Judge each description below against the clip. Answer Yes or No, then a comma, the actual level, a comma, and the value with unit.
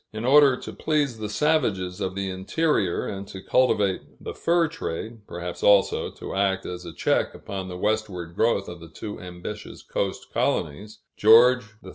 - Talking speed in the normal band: Yes, average, 175 wpm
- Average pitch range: Yes, average, 4.2 semitones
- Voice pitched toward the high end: No, low, 100 Hz